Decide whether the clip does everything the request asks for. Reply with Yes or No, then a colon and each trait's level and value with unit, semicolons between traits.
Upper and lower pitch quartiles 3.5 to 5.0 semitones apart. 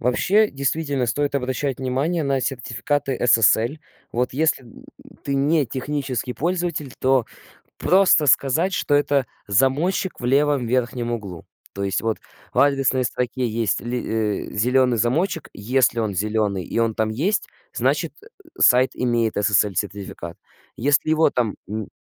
Yes: average, 3.9 semitones